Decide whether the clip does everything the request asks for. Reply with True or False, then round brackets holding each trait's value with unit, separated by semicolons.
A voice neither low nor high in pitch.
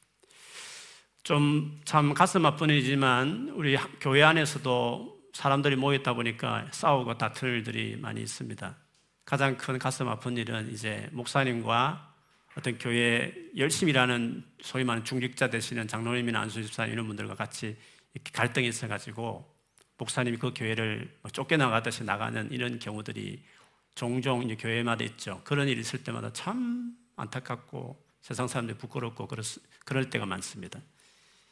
False (125 Hz)